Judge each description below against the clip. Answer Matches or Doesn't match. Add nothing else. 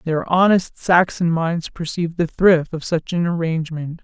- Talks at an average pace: Matches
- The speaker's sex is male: Doesn't match